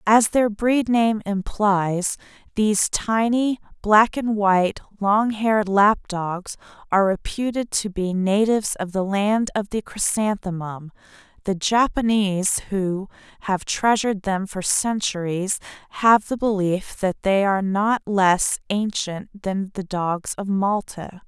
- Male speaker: No, female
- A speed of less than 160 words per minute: Yes, slow, 135 wpm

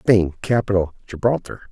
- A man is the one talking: Yes, male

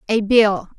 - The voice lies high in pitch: Yes, high, 210 Hz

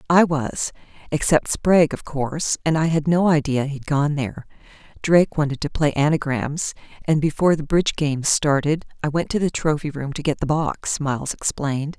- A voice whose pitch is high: No, medium, 150 Hz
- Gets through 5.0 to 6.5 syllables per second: Yes, 5.2 syllables/s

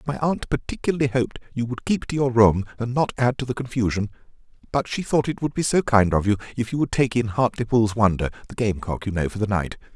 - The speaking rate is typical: No, fast, 240 wpm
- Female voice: No, male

